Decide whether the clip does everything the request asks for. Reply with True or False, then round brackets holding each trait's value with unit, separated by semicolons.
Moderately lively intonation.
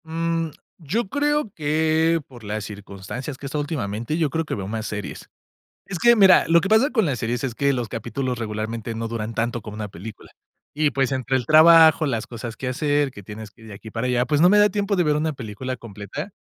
False (6.2 semitones)